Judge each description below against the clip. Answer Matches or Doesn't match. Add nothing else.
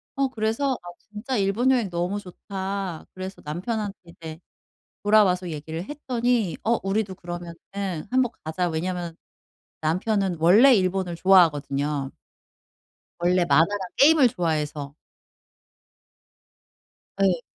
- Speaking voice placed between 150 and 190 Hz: Matches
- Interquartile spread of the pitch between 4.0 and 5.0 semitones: Matches